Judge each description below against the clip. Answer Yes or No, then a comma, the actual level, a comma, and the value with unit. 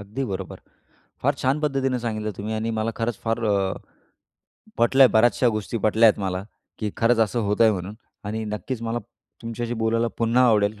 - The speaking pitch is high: No, low, 115 Hz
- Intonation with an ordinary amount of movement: No, narrow, 2.1 semitones